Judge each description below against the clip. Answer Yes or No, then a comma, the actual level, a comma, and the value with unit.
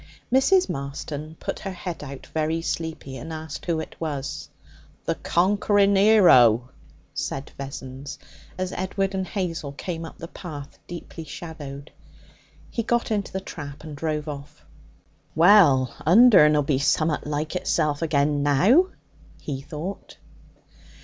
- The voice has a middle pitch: Yes, medium, 160 Hz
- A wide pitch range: No, average, 4.6 semitones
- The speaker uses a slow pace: Yes, slow, 130 wpm